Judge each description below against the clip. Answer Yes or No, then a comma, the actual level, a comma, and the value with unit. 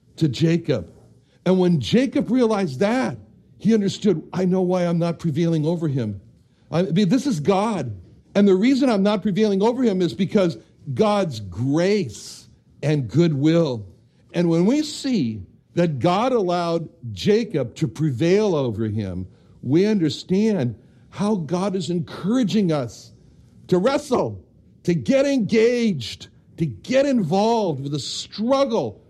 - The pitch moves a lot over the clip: Yes, wide, 7.3 semitones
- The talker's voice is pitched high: No, medium, 175 Hz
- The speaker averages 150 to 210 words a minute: No, slow, 135 wpm